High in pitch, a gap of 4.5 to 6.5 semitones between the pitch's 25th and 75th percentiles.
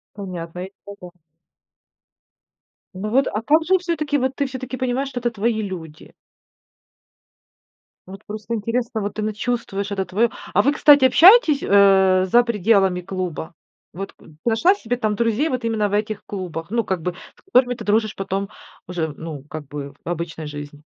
Yes: high, 210 Hz; average, 4.9 semitones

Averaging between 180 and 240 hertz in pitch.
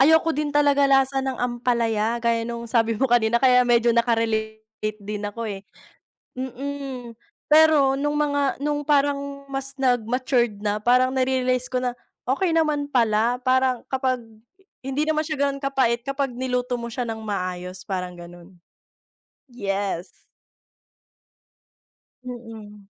No: very high, 250 Hz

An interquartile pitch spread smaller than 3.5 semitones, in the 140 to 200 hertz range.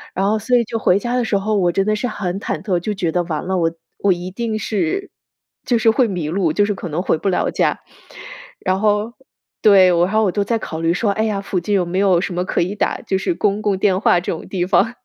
Yes: average, 3.1 semitones; high, 195 Hz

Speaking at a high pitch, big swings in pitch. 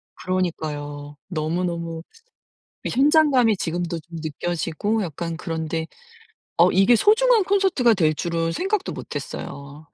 No: medium, 170 Hz; wide, 6.9 semitones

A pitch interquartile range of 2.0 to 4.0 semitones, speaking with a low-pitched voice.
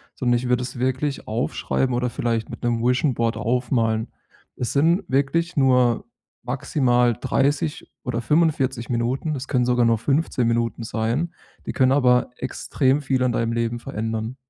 Yes: narrow, 2.4 semitones; low, 125 Hz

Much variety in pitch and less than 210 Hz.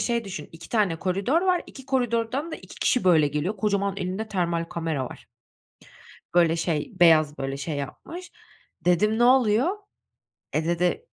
Yes: wide, 6.3 semitones; medium, 185 Hz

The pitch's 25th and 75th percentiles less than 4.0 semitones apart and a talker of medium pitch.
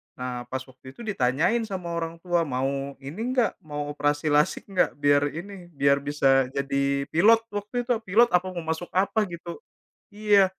No: wide, 5.6 semitones; medium, 160 Hz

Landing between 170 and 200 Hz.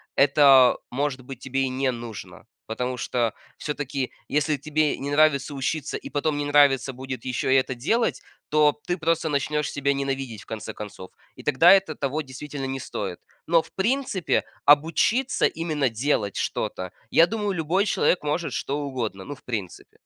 No: medium, 140 Hz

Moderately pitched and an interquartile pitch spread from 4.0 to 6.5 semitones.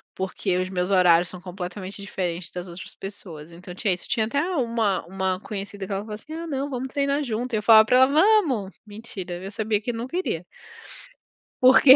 No: high, 205 Hz; average, 5.1 semitones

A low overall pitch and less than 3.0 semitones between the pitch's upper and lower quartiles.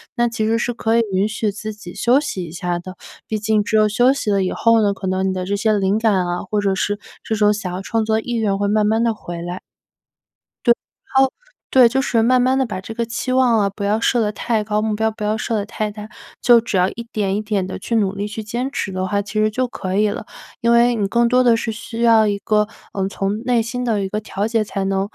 No: high, 215 Hz; narrow, 2.5 semitones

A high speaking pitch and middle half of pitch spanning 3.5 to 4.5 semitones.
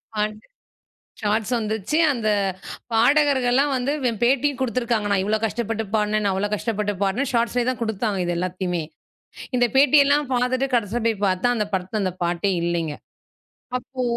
Yes: high, 220 Hz; average, 3.9 semitones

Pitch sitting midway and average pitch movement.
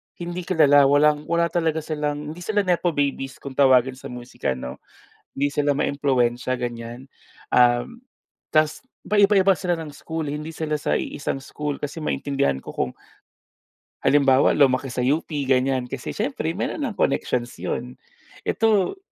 Yes: medium, 145 Hz; average, 3.9 semitones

